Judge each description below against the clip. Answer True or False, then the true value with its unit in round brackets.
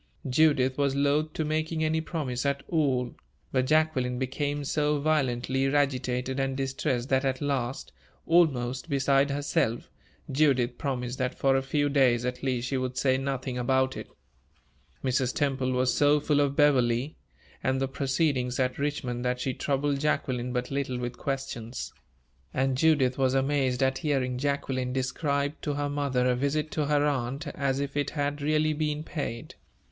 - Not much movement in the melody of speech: True (2.3 semitones)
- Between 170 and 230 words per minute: False (160 wpm)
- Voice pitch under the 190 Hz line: True (135 Hz)